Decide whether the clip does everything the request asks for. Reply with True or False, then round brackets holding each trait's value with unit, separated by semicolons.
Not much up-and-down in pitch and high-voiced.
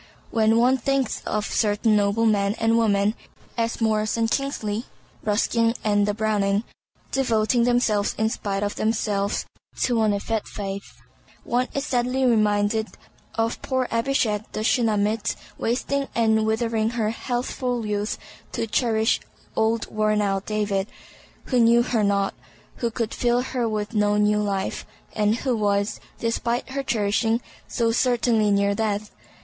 True (2.2 semitones; 220 Hz)